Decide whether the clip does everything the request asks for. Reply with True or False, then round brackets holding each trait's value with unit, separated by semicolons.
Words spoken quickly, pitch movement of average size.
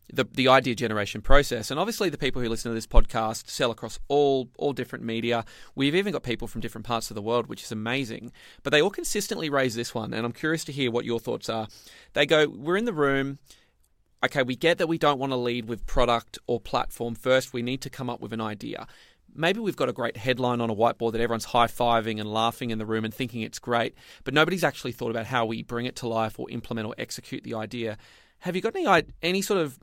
True (245 wpm; 3.2 semitones)